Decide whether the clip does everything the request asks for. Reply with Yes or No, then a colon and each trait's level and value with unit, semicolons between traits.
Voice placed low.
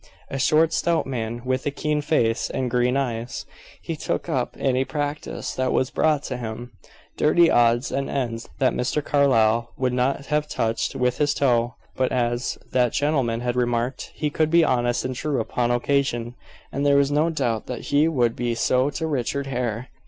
Yes: low, 130 Hz